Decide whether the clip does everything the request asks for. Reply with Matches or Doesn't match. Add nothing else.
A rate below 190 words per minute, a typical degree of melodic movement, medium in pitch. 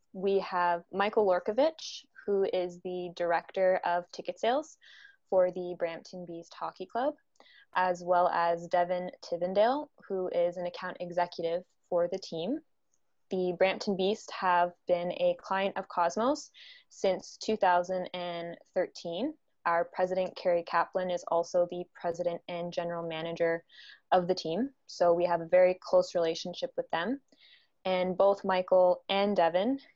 Doesn't match